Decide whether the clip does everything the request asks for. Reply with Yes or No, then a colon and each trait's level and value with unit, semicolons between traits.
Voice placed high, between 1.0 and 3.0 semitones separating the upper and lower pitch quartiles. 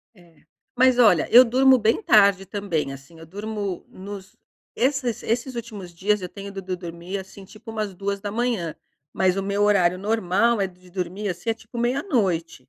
No: high, 200 Hz; average, 3.8 semitones